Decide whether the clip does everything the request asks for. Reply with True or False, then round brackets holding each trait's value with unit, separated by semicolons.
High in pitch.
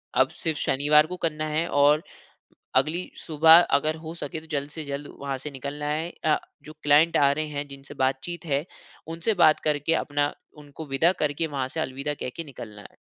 False (150 Hz)